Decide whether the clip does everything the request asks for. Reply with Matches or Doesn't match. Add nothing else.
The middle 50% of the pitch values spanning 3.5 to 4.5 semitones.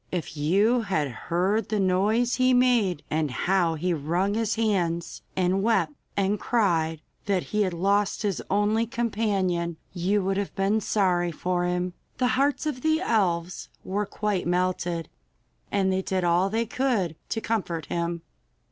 Matches